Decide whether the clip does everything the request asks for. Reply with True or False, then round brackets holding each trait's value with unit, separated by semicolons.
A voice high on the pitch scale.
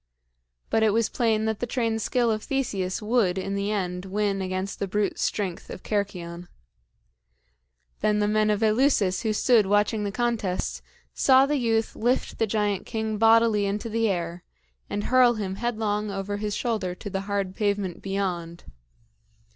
True (210 Hz)